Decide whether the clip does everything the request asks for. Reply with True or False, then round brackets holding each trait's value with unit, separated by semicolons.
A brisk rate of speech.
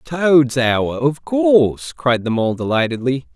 False (145 wpm)